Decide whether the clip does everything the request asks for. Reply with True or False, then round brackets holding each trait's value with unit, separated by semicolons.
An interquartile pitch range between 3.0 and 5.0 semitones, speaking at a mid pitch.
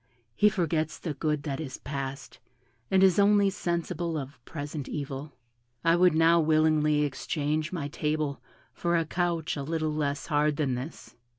False (2.6 semitones; 155 Hz)